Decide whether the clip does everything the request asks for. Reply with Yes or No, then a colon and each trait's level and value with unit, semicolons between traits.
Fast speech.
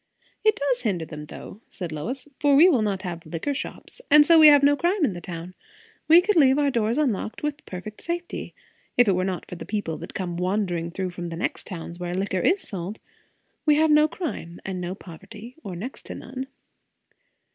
Yes: fast, 210 wpm